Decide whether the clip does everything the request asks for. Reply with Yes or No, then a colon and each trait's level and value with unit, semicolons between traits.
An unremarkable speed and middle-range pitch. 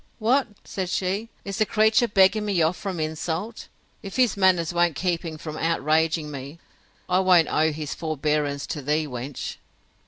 Yes: average, 165 wpm; medium, 170 Hz